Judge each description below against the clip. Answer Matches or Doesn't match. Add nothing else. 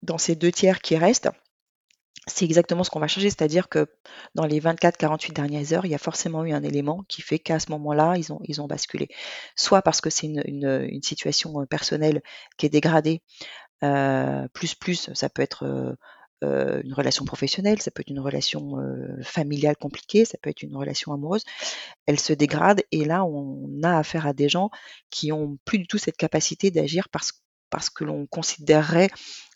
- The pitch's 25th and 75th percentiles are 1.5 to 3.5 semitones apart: Matches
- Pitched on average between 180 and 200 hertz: Doesn't match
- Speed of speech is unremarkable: Matches